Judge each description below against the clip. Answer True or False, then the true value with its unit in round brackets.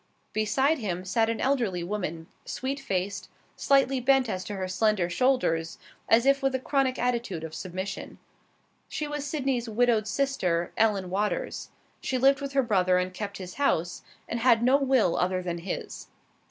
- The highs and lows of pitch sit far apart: True (6.3 semitones)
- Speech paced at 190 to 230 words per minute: False (165 wpm)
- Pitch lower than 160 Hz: False (225 Hz)